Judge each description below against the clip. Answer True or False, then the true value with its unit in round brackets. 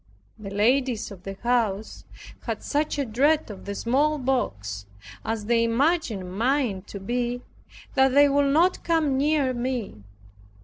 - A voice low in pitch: False (245 Hz)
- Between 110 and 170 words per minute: True (140 wpm)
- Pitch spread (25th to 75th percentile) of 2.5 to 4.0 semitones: False (5.2 semitones)